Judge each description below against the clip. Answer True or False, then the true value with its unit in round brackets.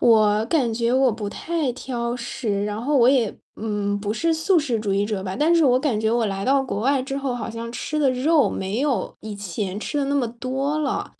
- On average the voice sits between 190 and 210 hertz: False (240 Hz)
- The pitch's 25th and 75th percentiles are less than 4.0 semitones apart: False (4.6 semitones)